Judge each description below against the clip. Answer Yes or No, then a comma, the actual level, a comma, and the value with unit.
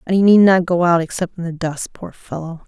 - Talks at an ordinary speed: No, fast, 270 wpm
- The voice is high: No, medium, 175 Hz